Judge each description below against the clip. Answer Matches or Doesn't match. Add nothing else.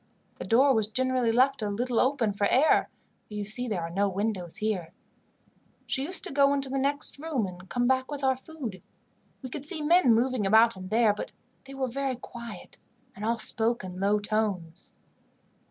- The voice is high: Matches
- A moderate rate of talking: Matches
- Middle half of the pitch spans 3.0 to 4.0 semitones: Doesn't match